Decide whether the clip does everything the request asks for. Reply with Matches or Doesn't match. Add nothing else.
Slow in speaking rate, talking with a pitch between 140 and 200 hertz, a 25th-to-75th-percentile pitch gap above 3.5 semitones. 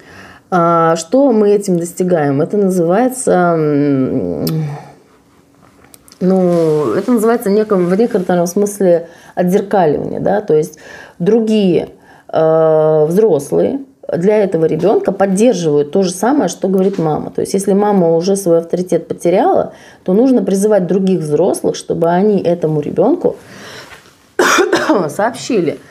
Matches